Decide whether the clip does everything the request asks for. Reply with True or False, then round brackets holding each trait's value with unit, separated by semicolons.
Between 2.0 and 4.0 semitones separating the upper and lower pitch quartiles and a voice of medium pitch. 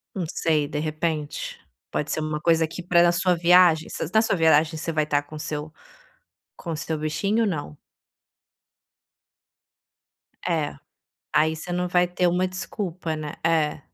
True (2.5 semitones; 160 Hz)